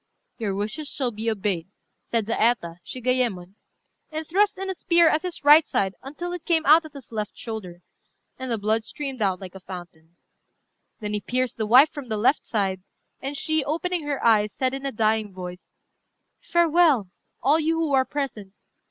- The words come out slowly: No, average, 185 wpm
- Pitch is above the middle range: Yes, high, 245 Hz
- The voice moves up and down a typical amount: No, wide, 6.6 semitones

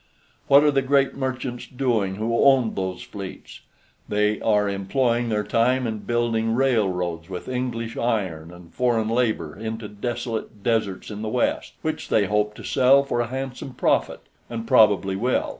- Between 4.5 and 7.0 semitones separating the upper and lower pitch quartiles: No, average, 3.4 semitones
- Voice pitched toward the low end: Yes, low, 115 Hz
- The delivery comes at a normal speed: Yes, average, 160 wpm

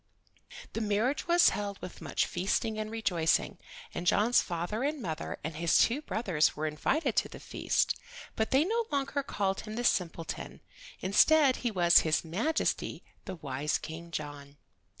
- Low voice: No, high, 200 Hz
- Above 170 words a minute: No, average, 160 wpm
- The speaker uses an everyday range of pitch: No, wide, 6.7 semitones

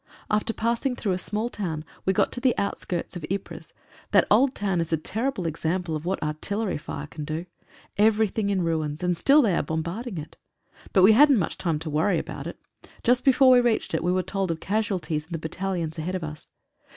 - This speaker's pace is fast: Yes, fast, 215 wpm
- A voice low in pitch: No, medium, 185 Hz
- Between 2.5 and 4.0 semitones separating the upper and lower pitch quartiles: No, average, 5.2 semitones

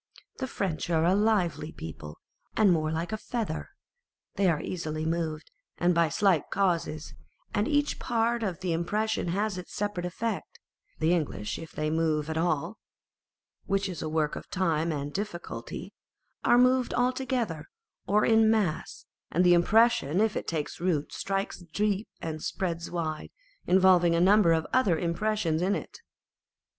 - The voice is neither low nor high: Yes, medium, 175 Hz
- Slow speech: No, average, 160 wpm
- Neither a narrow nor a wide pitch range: Yes, average, 4.6 semitones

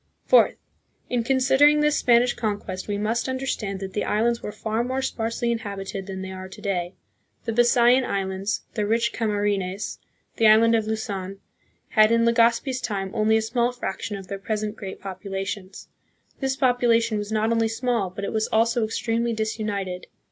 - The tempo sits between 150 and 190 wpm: Yes, average, 170 wpm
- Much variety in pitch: No, average, 3.0 semitones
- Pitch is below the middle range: No, high, 220 Hz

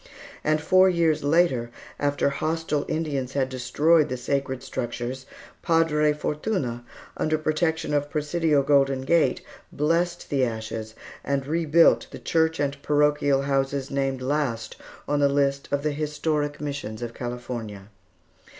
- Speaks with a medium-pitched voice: Yes, medium, 145 Hz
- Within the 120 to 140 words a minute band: Yes, slow, 135 wpm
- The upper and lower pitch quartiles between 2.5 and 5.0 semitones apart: Yes, average, 2.8 semitones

